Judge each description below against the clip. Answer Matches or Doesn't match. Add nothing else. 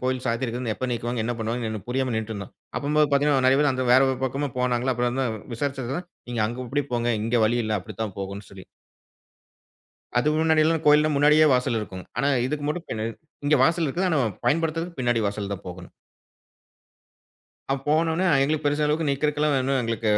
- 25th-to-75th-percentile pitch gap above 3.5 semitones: Matches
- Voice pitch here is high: Doesn't match